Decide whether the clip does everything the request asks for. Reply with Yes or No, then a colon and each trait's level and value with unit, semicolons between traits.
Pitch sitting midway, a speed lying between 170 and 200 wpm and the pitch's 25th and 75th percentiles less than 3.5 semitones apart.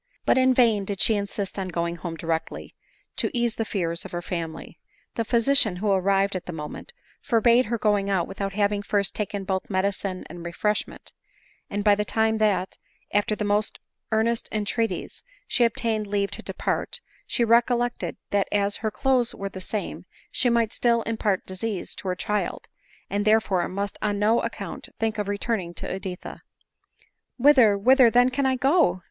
No: high, 205 Hz; average, 180 wpm; average, 3.0 semitones